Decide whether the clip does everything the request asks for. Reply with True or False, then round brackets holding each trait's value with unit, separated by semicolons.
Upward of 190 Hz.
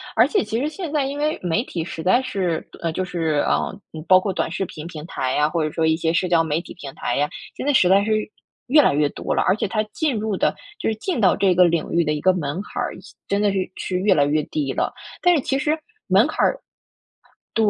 False (185 Hz)